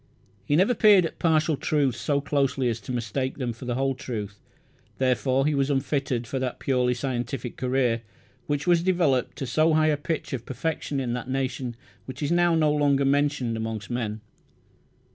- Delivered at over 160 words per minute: Yes, average, 180 wpm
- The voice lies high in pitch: No, low, 135 Hz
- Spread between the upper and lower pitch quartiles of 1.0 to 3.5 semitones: Yes, average, 3.2 semitones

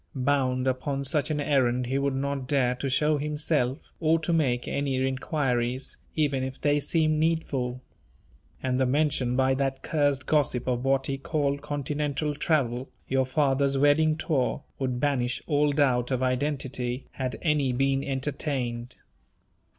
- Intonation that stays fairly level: Yes, narrow, 2.3 semitones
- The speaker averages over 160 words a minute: No, average, 150 wpm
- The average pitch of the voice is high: No, low, 135 Hz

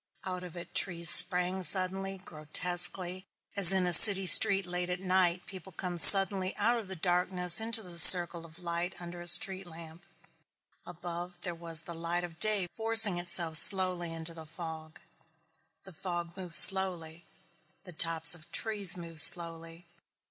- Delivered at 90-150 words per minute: No, average, 160 wpm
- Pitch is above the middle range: No, medium, 175 Hz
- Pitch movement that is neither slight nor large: No, narrow, 1.9 semitones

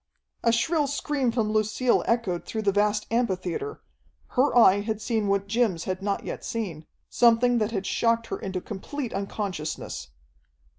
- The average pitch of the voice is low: No, high, 215 Hz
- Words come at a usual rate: Yes, average, 155 wpm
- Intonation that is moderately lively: Yes, average, 3.2 semitones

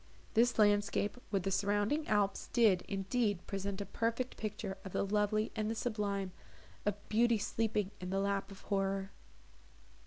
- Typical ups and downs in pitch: No, narrow, 1.8 semitones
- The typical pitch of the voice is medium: No, high, 205 Hz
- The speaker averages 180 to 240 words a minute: No, average, 155 wpm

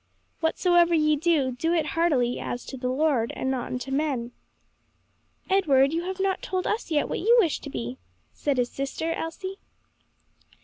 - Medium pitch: No, very high, 305 Hz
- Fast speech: No, average, 170 wpm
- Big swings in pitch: No, average, 4.8 semitones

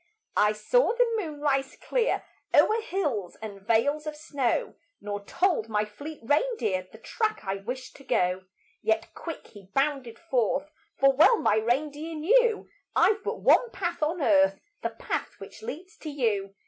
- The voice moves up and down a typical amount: No, wide, 8.2 semitones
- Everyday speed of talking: Yes, average, 160 wpm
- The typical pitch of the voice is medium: No, very high, 280 Hz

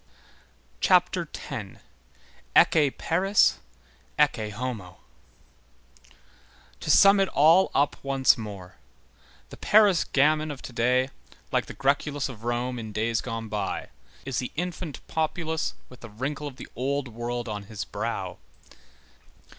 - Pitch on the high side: No, low, 130 Hz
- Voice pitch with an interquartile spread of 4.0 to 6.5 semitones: Yes, average, 5.1 semitones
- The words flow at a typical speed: No, slow, 125 wpm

